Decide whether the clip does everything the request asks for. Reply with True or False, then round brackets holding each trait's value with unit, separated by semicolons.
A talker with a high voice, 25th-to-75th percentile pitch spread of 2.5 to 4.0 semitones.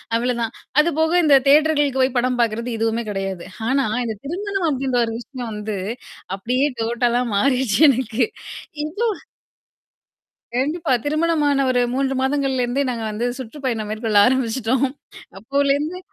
True (260 Hz; 3.5 semitones)